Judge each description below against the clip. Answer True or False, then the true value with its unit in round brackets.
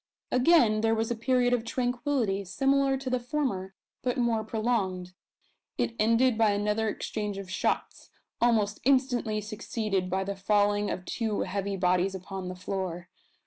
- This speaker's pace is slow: False (150 wpm)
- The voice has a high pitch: True (215 Hz)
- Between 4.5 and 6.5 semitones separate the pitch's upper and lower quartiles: False (4.0 semitones)